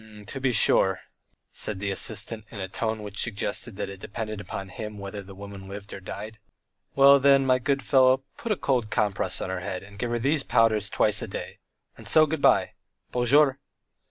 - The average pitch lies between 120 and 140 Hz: No, low, 110 Hz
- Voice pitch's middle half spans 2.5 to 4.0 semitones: No, average, 4.7 semitones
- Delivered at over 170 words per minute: Yes, average, 200 wpm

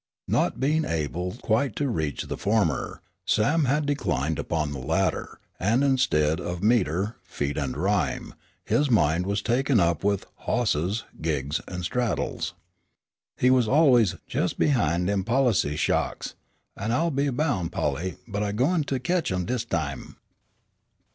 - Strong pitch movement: Yes, wide, 7.7 semitones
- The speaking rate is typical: Yes, average, 150 wpm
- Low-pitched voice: Yes, low, 100 Hz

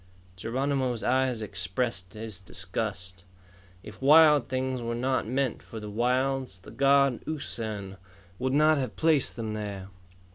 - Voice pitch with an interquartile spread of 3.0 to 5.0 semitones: Yes, average, 4.4 semitones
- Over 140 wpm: No, slow, 135 wpm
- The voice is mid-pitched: No, low, 120 Hz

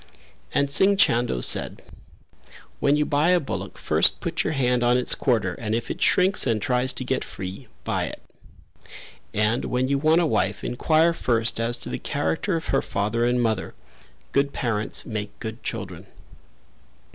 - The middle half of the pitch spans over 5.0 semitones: No, average, 4.2 semitones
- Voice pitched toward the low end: Yes, low, 125 Hz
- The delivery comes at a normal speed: Yes, average, 170 wpm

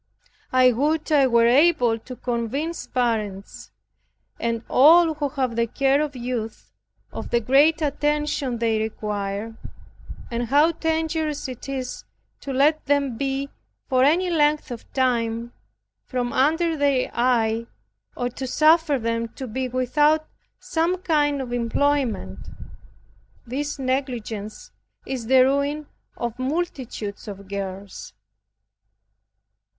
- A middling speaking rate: No, slow, 120 wpm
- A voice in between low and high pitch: No, very high, 260 Hz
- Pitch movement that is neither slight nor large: Yes, average, 4.1 semitones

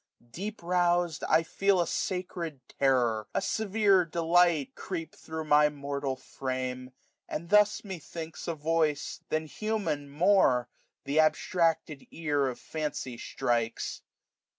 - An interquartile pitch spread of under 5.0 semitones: Yes, average, 4.0 semitones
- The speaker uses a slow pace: Yes, slow, 130 wpm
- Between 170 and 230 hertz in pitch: No, medium, 160 Hz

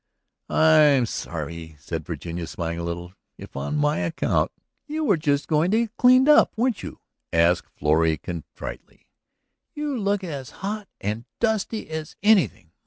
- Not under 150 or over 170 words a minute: Yes, average, 160 wpm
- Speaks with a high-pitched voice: No, medium, 150 Hz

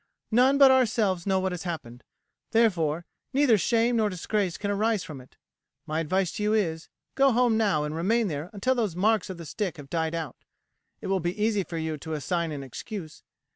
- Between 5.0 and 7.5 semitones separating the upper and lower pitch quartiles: Yes, average, 5.3 semitones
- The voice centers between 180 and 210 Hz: Yes, high, 190 Hz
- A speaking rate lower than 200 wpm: No, fast, 205 wpm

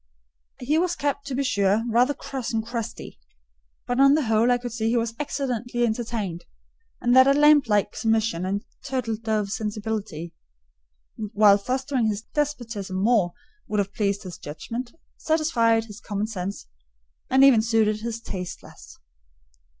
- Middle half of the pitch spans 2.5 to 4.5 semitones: Yes, average, 3.3 semitones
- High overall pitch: Yes, high, 225 Hz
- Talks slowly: No, average, 155 wpm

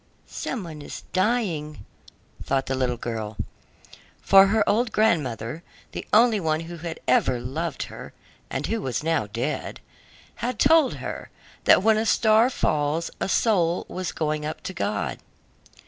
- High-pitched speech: No, medium, 165 Hz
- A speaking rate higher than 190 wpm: No, average, 150 wpm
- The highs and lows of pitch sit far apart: Yes, wide, 7.9 semitones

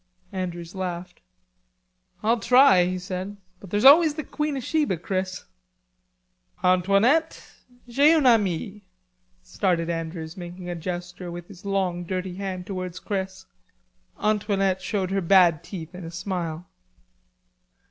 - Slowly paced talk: Yes, slow, 125 wpm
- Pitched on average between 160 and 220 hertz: Yes, medium, 185 Hz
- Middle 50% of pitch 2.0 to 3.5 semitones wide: Yes, average, 2.8 semitones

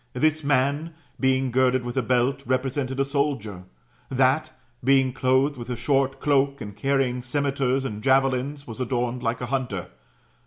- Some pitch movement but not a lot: No, narrow, 1.8 semitones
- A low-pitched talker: Yes, low, 130 Hz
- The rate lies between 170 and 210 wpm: No, average, 155 wpm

